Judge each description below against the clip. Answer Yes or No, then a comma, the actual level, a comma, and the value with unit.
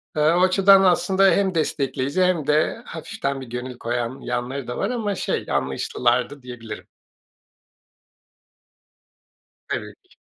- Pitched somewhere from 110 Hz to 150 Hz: Yes, medium, 140 Hz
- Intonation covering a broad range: Yes, wide, 7.1 semitones